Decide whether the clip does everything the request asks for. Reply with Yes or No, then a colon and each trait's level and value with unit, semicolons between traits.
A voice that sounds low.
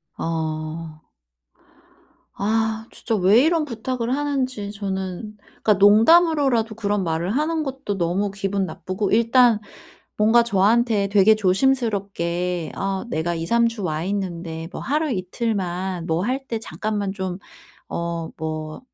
No: high, 205 Hz